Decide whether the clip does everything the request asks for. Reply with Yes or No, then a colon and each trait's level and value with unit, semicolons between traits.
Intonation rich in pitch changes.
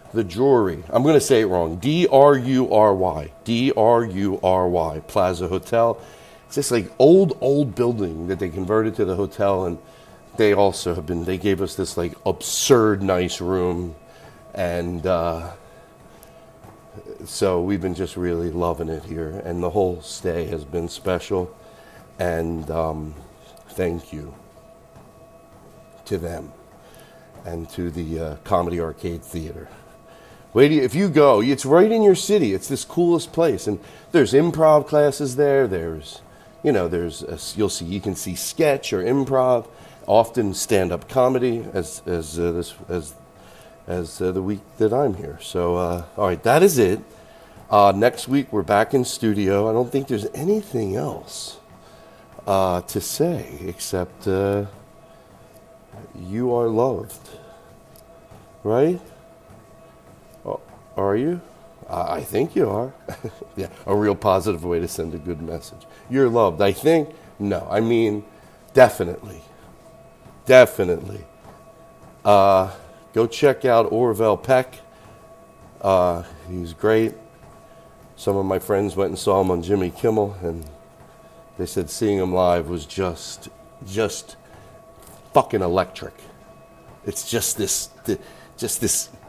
Yes: wide, 6.6 semitones